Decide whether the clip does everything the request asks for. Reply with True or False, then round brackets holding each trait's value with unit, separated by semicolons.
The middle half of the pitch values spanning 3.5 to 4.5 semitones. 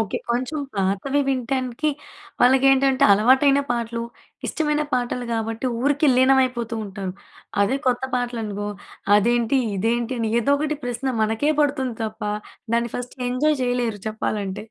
False (3.0 semitones)